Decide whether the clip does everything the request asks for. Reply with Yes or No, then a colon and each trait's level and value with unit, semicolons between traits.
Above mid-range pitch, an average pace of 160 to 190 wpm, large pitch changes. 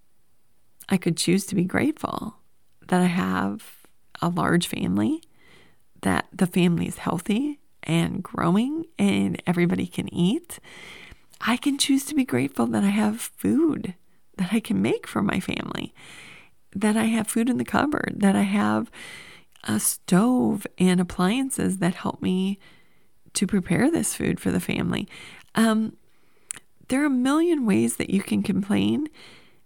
No: high, 200 Hz; average, 150 wpm; wide, 5.8 semitones